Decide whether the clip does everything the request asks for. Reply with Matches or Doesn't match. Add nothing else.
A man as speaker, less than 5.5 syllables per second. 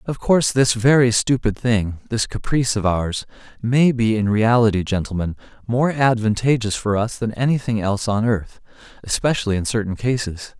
Matches